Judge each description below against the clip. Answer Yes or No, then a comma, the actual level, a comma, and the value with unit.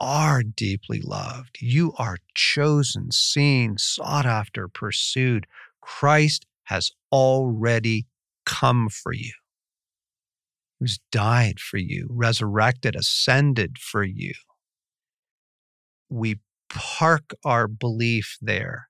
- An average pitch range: Yes, average, 3.9 semitones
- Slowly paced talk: Yes, slow, 90 wpm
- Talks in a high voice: No, low, 125 Hz